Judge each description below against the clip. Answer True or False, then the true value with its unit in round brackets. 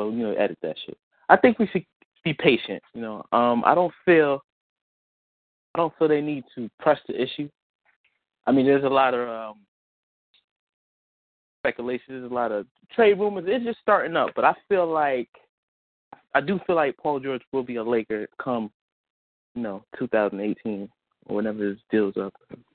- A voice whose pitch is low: True (125 Hz)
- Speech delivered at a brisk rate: False (175 wpm)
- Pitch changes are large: True (6.1 semitones)